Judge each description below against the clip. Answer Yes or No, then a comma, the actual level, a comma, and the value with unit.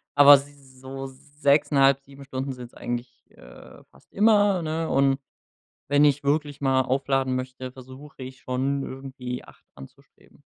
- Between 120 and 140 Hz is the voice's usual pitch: Yes, low, 135 Hz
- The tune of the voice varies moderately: No, narrow, 1.7 semitones